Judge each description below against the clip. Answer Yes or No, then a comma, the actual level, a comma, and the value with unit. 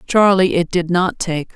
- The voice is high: No, medium, 175 Hz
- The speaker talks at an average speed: Yes, average, 195 wpm